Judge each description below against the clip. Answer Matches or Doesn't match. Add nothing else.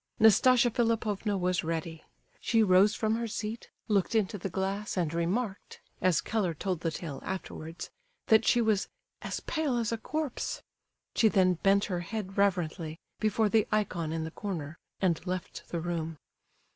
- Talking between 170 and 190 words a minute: Doesn't match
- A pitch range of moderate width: Matches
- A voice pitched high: Matches